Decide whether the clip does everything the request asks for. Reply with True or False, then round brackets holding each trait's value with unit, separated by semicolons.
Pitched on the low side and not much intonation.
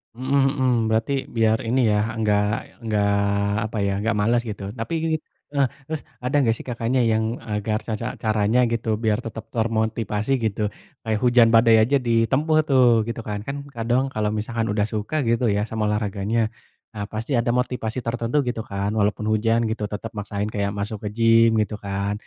True (110 Hz; 1.9 semitones)